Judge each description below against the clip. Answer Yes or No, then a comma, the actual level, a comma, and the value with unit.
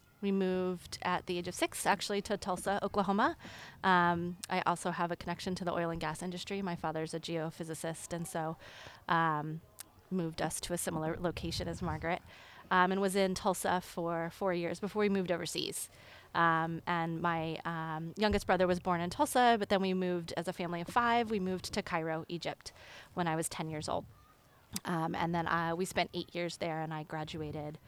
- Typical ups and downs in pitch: No, narrow, 2.2 semitones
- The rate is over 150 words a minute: Yes, average, 200 wpm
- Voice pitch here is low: No, medium, 175 Hz